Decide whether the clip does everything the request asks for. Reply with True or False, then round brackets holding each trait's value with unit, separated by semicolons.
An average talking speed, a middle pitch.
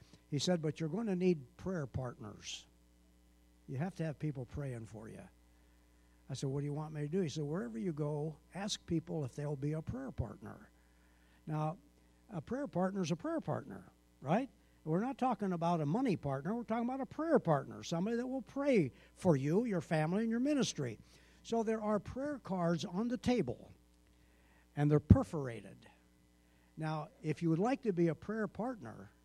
True (190 wpm; 155 Hz)